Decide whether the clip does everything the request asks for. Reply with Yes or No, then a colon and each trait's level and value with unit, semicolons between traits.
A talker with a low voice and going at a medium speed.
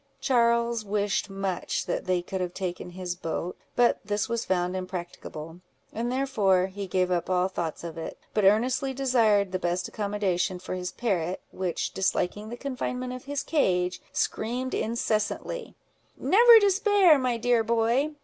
No: high, 205 Hz; average, 150 wpm